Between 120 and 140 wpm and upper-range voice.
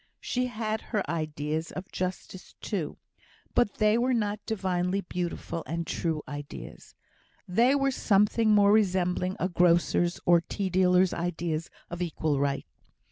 No: slow, 135 wpm; medium, 180 Hz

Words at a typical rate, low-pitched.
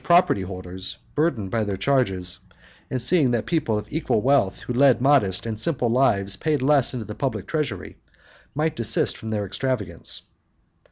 Yes: average, 165 wpm; low, 120 Hz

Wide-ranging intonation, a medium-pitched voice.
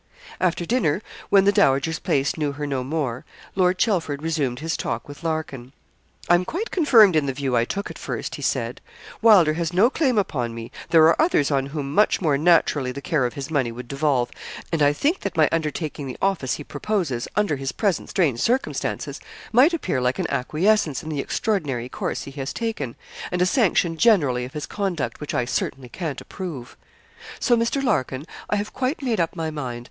Yes: wide, 6.2 semitones; medium, 155 Hz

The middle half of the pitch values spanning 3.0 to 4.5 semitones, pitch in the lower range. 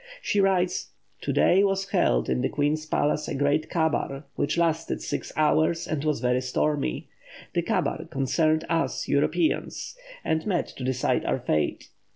No: average, 3.4 semitones; medium, 155 Hz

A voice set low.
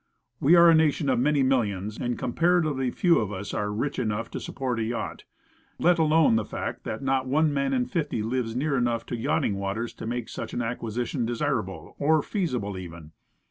Yes: low, 125 Hz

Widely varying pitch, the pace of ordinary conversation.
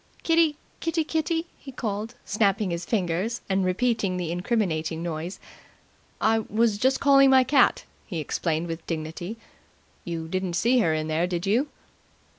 Yes: wide, 6.4 semitones; average, 150 wpm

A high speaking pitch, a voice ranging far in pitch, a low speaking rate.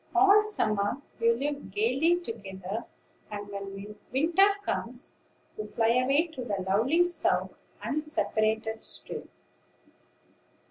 Yes: high, 230 Hz; wide, 6.6 semitones; slow, 105 wpm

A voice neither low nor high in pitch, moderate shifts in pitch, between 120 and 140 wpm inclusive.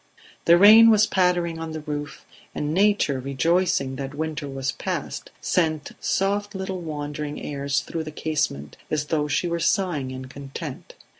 No: medium, 155 Hz; average, 4.1 semitones; average, 155 wpm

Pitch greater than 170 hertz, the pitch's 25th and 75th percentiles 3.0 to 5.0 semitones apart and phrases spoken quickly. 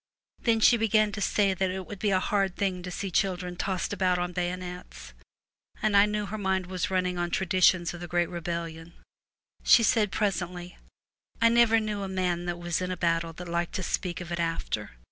No: medium, 185 Hz; narrow, 2.5 semitones; fast, 215 wpm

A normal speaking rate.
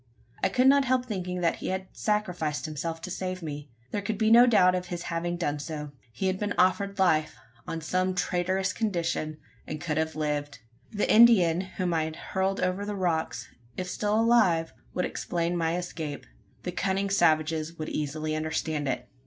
Yes: average, 185 wpm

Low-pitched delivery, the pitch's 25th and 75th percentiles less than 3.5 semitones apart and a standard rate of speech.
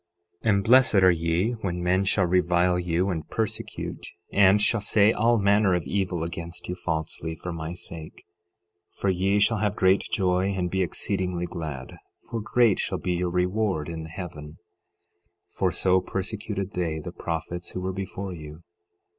Yes: very low, 90 Hz; average, 2.7 semitones; average, 170 wpm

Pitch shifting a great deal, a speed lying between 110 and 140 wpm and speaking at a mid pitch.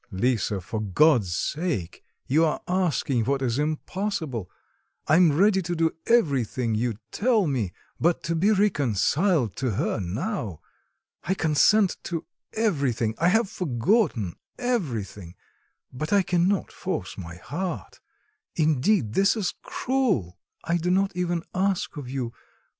Yes: wide, 8.3 semitones; slow, 135 wpm; medium, 155 Hz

